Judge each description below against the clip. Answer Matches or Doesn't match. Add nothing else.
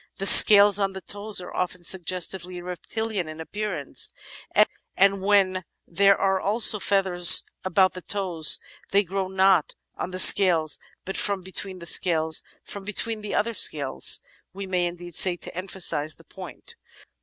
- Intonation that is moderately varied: Doesn't match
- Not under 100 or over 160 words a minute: Matches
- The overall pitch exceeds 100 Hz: Matches